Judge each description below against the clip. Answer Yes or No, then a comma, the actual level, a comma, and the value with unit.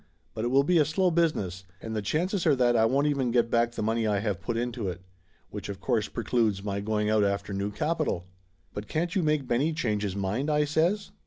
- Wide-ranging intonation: Yes, wide, 6.5 semitones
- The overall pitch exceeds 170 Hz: No, low, 115 Hz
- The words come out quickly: Yes, fast, 235 wpm